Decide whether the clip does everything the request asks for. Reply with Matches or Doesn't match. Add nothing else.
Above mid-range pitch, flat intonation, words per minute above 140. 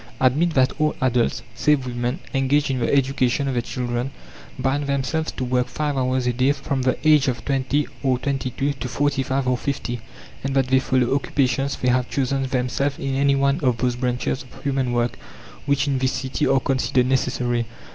Doesn't match